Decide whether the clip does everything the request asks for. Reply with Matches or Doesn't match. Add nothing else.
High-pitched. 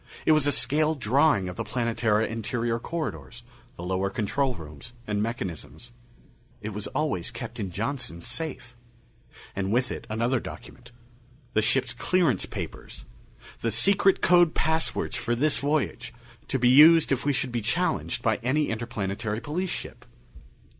Doesn't match